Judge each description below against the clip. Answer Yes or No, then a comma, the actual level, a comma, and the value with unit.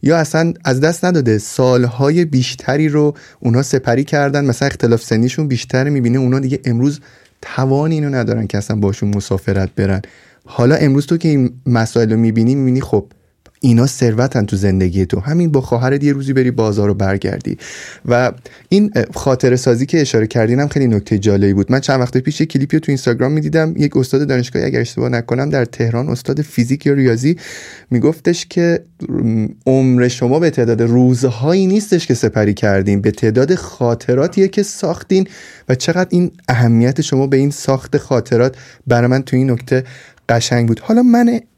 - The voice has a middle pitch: No, low, 130 Hz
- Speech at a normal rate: No, fast, 170 wpm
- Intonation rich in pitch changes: No, average, 3.8 semitones